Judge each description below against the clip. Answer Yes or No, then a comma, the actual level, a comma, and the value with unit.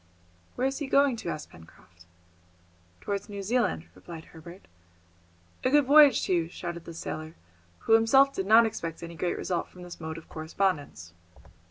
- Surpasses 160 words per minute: Yes, average, 170 wpm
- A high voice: No, medium, 180 Hz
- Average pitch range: No, wide, 6.0 semitones